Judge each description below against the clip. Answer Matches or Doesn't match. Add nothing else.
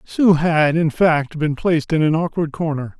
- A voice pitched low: Doesn't match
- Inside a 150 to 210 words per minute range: Matches